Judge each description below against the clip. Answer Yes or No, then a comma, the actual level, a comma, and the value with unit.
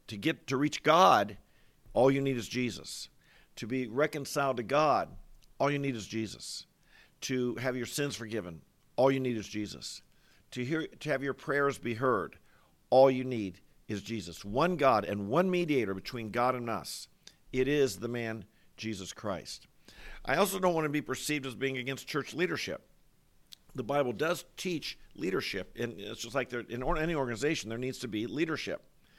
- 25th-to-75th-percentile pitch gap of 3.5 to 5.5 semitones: Yes, average, 4.0 semitones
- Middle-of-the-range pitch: No, low, 130 Hz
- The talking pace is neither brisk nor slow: Yes, average, 180 wpm